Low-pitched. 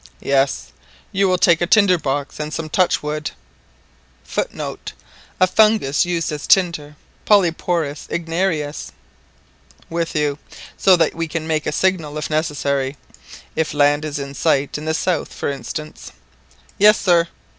No: medium, 160 Hz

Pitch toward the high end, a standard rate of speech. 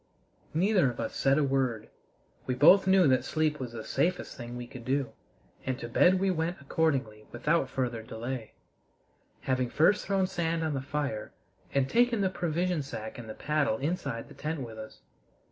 No: medium, 140 Hz; average, 180 wpm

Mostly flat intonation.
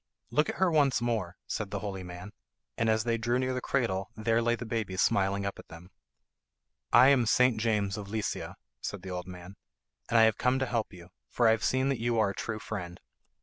No: average, 3.5 semitones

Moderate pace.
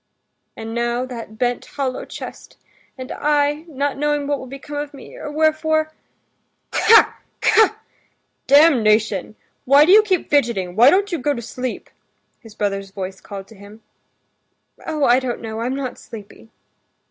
Yes: average, 155 wpm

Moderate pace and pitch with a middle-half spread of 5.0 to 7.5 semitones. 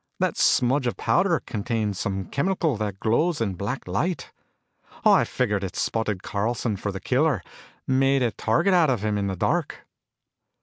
Yes: average, 165 wpm; average, 5.3 semitones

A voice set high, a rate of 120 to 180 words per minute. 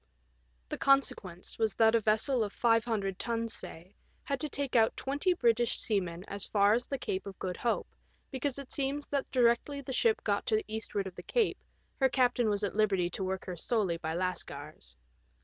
No: high, 225 Hz; average, 200 wpm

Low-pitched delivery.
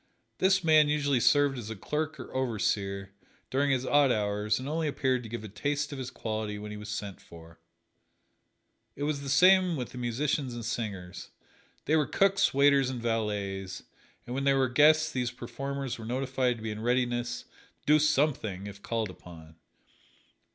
Yes: low, 125 Hz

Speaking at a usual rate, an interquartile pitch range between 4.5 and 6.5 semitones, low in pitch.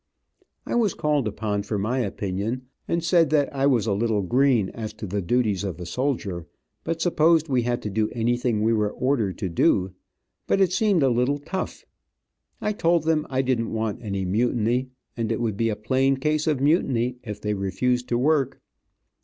Yes: average, 195 wpm; average, 5.1 semitones; low, 120 Hz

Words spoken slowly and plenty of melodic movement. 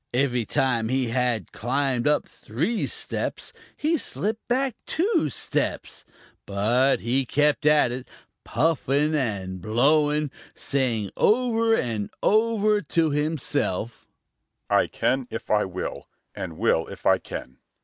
Yes: slow, 125 wpm; wide, 5.7 semitones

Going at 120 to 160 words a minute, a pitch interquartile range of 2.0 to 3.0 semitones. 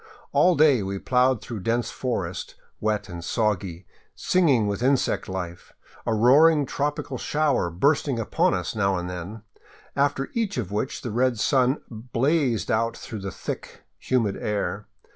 No: average, 150 wpm; wide, 5.5 semitones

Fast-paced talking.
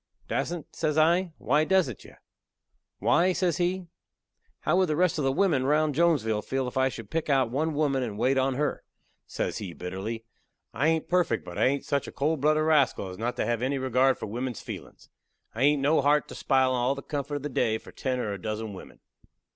Yes: fast, 220 wpm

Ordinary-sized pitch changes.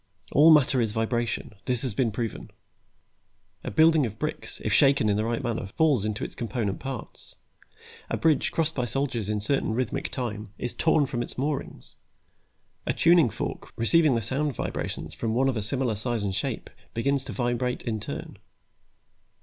Yes: average, 4.0 semitones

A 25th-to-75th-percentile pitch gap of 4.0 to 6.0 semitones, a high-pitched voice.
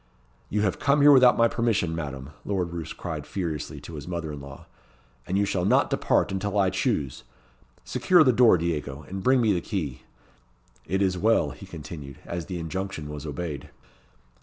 No: average, 5.1 semitones; very low, 90 Hz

